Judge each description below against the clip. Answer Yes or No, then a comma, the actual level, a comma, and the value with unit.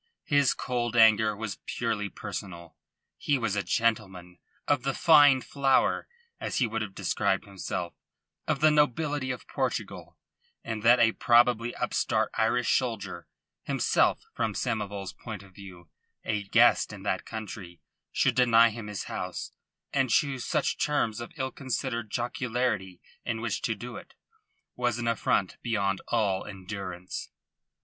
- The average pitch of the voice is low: Yes, low, 115 Hz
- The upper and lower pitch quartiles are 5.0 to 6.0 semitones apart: No, average, 3.7 semitones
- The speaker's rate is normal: Yes, average, 145 wpm